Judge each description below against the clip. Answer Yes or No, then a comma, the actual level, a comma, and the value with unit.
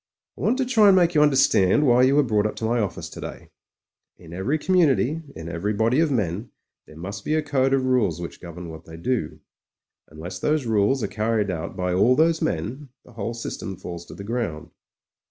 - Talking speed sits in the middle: No, fast, 220 wpm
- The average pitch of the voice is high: No, low, 115 Hz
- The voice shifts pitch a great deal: Yes, wide, 7.4 semitones